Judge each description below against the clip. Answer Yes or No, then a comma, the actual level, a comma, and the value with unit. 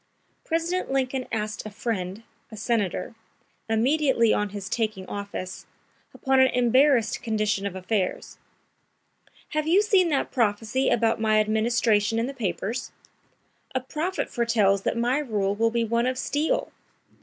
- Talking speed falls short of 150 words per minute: Yes, average, 140 wpm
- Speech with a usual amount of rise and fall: Yes, average, 3.8 semitones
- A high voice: Yes, high, 230 Hz